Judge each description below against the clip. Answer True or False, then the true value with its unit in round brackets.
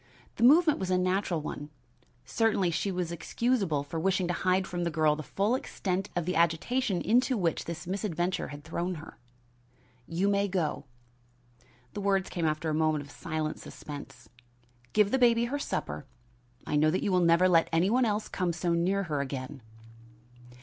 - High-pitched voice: False (180 Hz)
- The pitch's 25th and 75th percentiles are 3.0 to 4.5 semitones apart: True (4.0 semitones)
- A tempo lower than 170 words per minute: False (180 wpm)